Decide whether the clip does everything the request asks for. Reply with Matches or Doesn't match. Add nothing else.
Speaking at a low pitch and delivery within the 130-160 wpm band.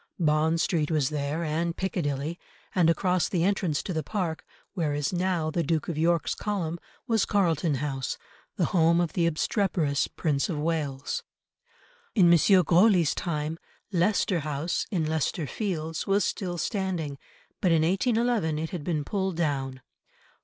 Doesn't match